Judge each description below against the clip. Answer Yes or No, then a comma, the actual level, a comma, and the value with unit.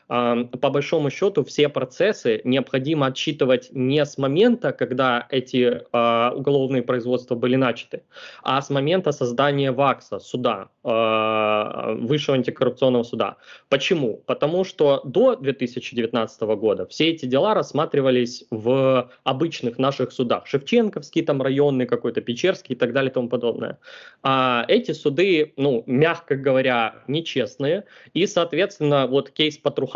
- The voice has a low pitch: Yes, low, 130 Hz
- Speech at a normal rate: Yes, average, 125 wpm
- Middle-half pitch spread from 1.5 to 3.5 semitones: Yes, narrow, 2.6 semitones